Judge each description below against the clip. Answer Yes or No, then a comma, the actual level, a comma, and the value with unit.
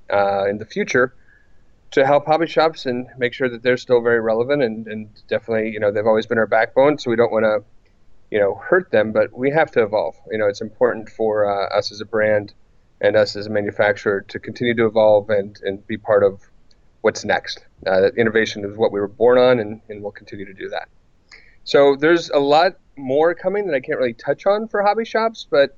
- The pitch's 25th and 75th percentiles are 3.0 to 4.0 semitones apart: No, average, 5.2 semitones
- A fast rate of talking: Yes, fast, 230 wpm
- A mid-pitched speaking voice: No, low, 115 Hz